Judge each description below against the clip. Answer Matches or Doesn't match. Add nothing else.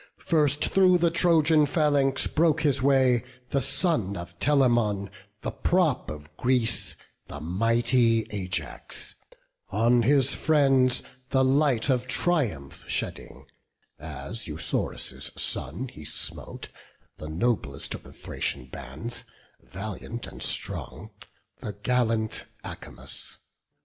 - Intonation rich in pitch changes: Matches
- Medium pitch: Doesn't match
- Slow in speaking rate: Matches